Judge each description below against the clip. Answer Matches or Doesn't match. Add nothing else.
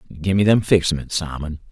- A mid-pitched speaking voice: Doesn't match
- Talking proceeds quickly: Matches